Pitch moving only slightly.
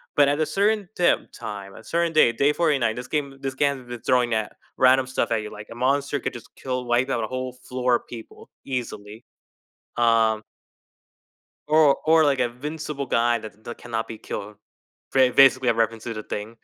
No: average, 3.4 semitones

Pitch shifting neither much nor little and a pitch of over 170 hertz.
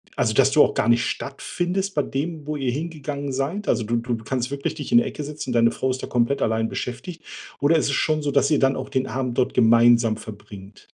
No: average, 4.2 semitones; low, 135 Hz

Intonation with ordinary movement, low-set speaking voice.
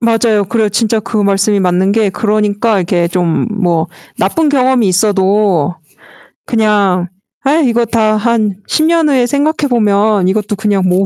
No: average, 3.3 semitones; high, 210 Hz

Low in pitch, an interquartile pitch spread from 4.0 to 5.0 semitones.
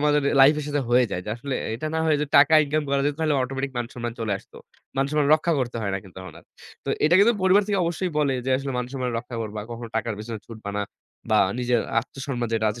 Yes: low, 130 Hz; average, 4.3 semitones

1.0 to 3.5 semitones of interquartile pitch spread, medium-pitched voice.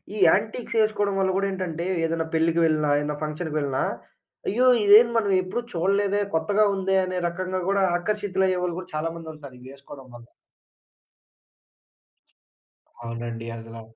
No: average, 4.6 semitones; medium, 180 Hz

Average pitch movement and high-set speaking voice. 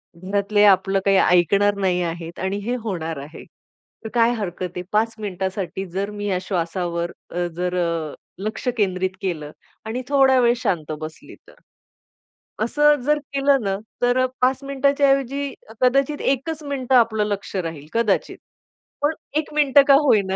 No: wide, 6.4 semitones; high, 205 Hz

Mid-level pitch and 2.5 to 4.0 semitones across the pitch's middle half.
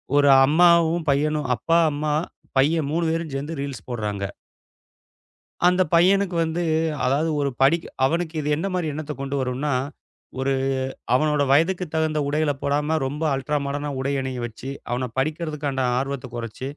Yes: medium, 150 Hz; average, 3.0 semitones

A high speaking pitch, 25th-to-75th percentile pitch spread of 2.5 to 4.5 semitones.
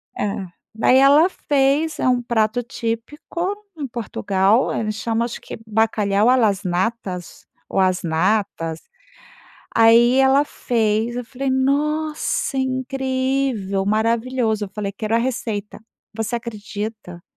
Yes: high, 230 Hz; average, 4.0 semitones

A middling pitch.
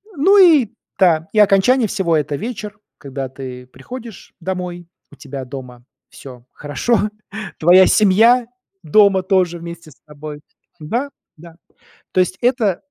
Yes: medium, 180 Hz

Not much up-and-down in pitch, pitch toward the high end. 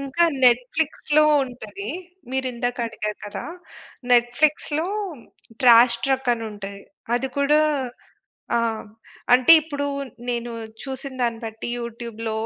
No: average, 3.0 semitones; high, 245 Hz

